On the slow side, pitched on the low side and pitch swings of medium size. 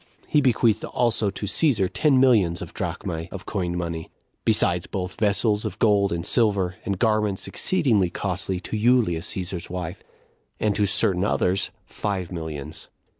No: average, 150 wpm; low, 100 Hz; average, 3.5 semitones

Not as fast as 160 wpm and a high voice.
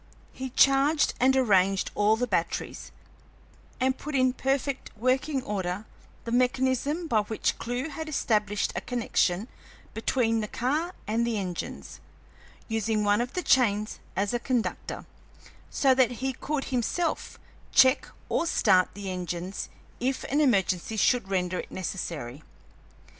Yes: slow, 135 wpm; high, 235 Hz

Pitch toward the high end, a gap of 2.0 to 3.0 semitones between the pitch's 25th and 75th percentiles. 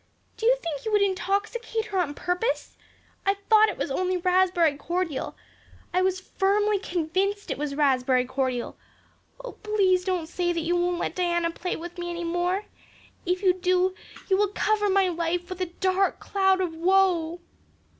Yes: very high, 365 Hz; narrow, 2.5 semitones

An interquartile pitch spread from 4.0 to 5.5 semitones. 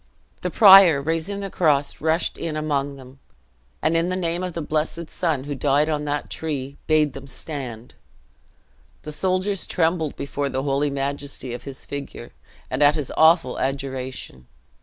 No: average, 3.0 semitones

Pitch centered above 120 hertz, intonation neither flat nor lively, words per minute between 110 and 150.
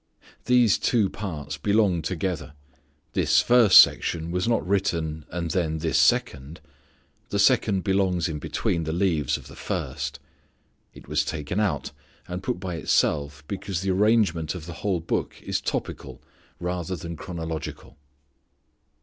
No: very low, 90 Hz; average, 3.8 semitones; average, 140 wpm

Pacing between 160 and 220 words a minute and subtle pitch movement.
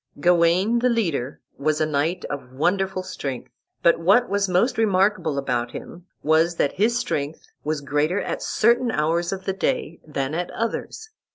No: average, 165 wpm; average, 5.1 semitones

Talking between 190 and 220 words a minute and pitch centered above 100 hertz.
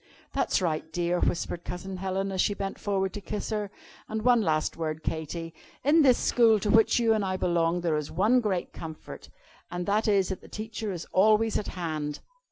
Yes: average, 200 wpm; high, 190 Hz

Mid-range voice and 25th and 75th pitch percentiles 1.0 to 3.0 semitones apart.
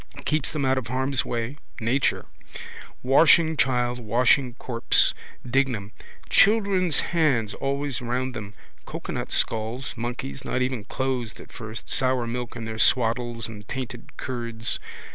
No: low, 125 Hz; narrow, 2.6 semitones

